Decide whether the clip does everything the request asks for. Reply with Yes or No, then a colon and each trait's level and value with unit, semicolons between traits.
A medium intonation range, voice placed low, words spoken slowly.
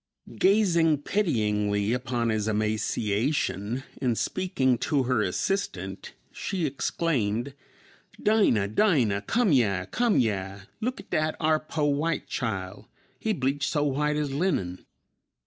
No: wide, 7.1 semitones; low, 130 Hz; slow, 120 wpm